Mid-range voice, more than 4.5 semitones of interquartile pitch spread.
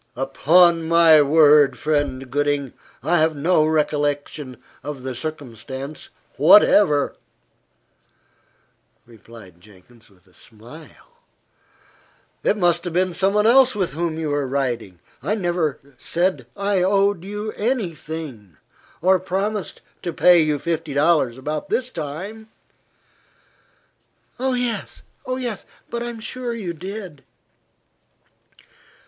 Yes: medium, 160 Hz; wide, 5.5 semitones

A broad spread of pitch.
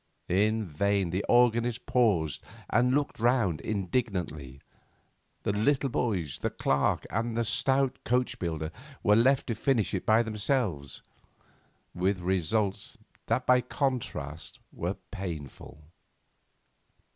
Yes: wide, 5.7 semitones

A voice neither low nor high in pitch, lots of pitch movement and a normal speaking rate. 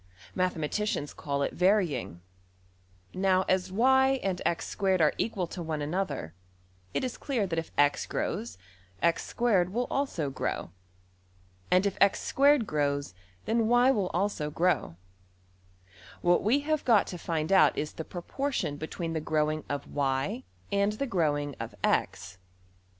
No: medium, 180 Hz; wide, 6.1 semitones; slow, 120 wpm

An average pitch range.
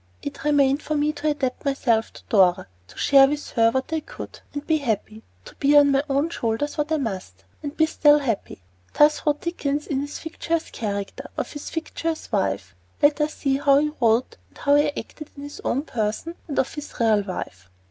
Yes: average, 4.6 semitones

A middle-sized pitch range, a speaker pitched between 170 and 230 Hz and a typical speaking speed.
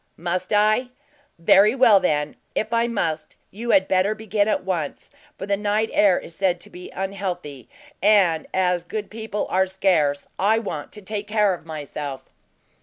Yes: average, 3.5 semitones; high, 190 Hz; average, 170 wpm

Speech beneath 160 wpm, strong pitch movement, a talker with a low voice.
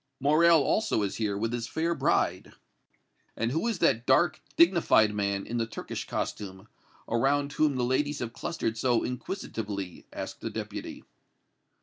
Yes: average, 150 wpm; wide, 5.7 semitones; low, 120 Hz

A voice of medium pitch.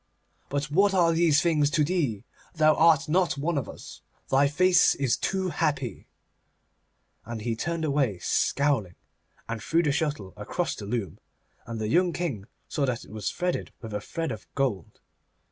Yes: medium, 145 Hz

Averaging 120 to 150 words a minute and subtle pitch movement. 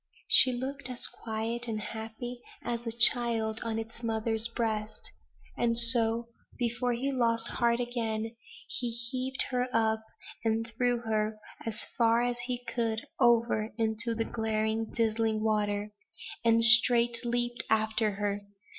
Yes: slow, 135 wpm; narrow, 1.4 semitones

